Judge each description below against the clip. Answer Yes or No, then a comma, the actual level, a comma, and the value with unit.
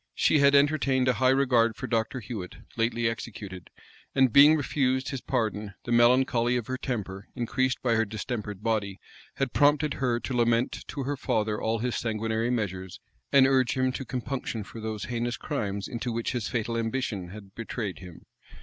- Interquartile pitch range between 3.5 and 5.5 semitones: No, average, 3.1 semitones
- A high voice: No, low, 120 Hz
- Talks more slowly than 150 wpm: No, average, 175 wpm